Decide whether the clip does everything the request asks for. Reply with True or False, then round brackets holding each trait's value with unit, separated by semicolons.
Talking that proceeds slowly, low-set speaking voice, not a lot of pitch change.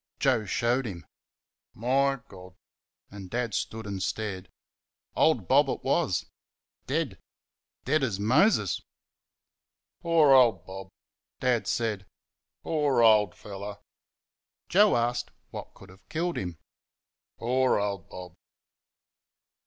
False (110 wpm; 115 Hz; 5.6 semitones)